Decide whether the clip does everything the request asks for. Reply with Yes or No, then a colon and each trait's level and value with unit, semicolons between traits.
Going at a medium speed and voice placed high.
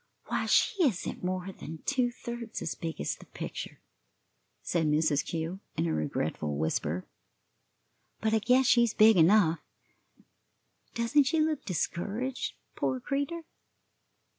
No: slow, 130 wpm; high, 210 Hz